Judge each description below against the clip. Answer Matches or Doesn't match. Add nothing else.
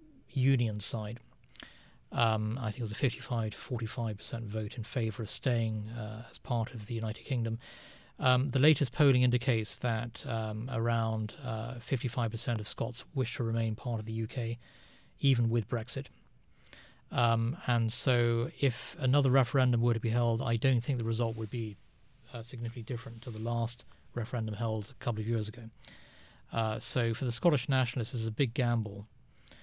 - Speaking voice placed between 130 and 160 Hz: Doesn't match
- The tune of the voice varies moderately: Doesn't match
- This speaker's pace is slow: Doesn't match